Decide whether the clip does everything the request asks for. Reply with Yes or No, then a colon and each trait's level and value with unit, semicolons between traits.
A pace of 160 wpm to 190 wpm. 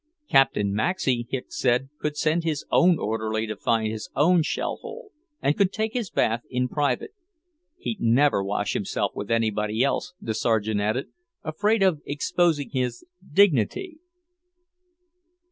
No: average, 145 wpm